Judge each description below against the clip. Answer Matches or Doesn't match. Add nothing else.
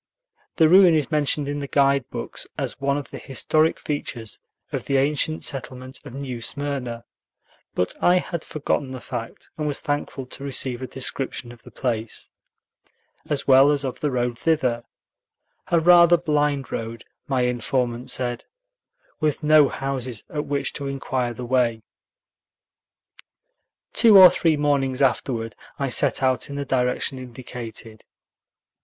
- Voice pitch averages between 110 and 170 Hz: Matches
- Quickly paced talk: Doesn't match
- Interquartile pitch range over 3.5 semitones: Doesn't match